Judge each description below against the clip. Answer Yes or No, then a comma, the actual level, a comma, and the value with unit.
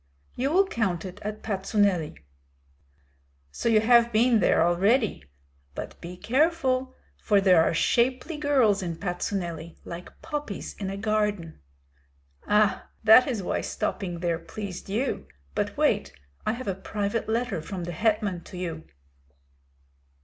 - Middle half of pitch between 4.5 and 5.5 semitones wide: Yes, average, 4.8 semitones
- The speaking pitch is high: Yes, high, 205 Hz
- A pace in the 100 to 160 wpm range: Yes, average, 140 wpm